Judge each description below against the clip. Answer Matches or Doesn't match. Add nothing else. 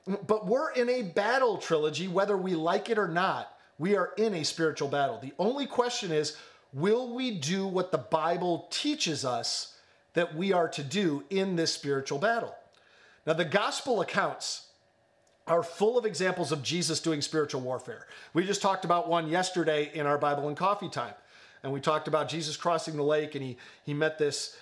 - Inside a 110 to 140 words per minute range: Doesn't match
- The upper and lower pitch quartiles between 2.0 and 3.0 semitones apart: Doesn't match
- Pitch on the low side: Doesn't match